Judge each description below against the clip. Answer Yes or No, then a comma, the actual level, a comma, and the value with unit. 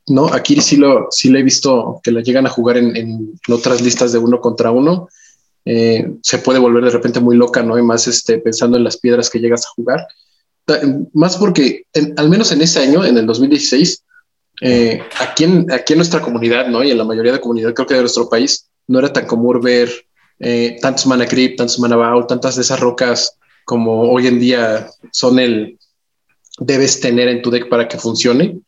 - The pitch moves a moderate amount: No, narrow, 2.2 semitones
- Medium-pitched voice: No, low, 125 Hz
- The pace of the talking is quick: Yes, fast, 215 wpm